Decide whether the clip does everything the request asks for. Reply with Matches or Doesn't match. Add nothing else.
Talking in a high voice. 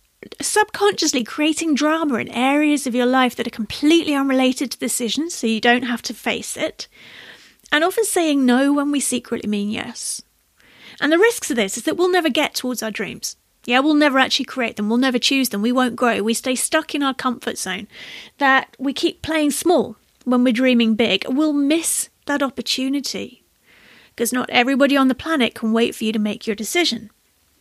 Matches